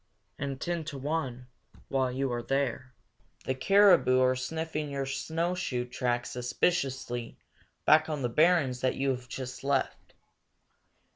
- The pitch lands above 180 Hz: No, low, 135 Hz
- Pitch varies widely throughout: No, average, 3.6 semitones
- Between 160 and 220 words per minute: No, slow, 135 wpm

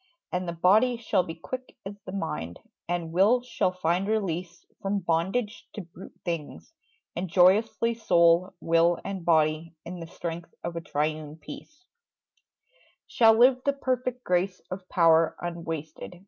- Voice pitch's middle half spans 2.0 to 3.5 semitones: No, average, 4.3 semitones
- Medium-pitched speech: Yes, medium, 180 Hz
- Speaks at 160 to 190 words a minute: No, average, 145 wpm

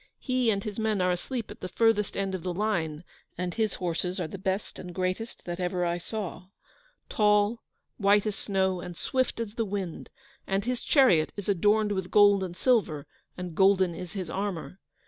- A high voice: Yes, high, 195 Hz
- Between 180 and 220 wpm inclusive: Yes, average, 190 wpm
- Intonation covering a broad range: No, average, 2.9 semitones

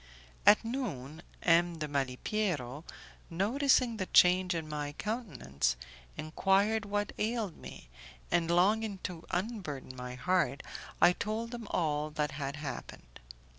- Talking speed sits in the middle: No, slow, 125 wpm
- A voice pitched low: No, medium, 175 Hz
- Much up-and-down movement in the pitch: Yes, wide, 6.4 semitones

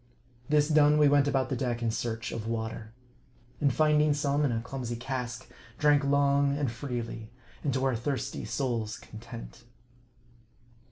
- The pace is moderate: Yes, average, 155 wpm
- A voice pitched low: Yes, low, 130 Hz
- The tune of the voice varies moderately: Yes, average, 3.6 semitones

